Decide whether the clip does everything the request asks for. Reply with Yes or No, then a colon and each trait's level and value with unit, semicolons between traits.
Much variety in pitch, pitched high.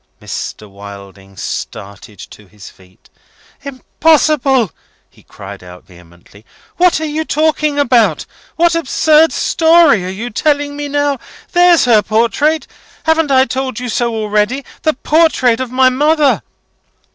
Yes: wide, 6.9 semitones; very high, 260 Hz